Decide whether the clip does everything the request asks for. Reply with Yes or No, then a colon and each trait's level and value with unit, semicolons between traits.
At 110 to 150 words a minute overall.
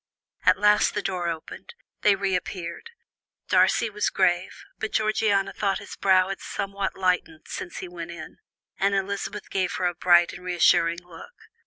No: average, 160 wpm